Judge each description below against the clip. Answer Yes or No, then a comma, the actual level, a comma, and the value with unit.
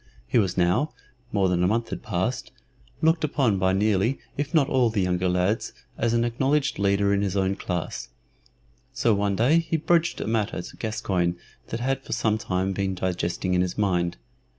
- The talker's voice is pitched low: Yes, low, 100 Hz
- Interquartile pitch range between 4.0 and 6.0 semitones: Yes, average, 4.4 semitones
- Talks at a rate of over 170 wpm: Yes, average, 195 wpm